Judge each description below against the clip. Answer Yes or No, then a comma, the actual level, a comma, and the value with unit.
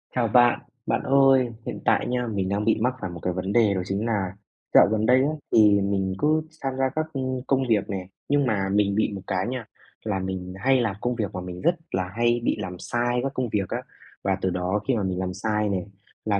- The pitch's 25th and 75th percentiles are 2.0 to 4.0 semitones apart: No, average, 4.5 semitones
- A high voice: No, low, 105 Hz